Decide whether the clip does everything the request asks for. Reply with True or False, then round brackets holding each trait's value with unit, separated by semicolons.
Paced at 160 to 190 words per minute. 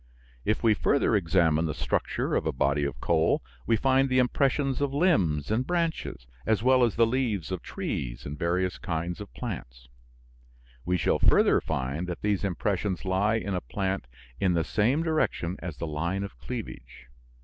True (175 wpm)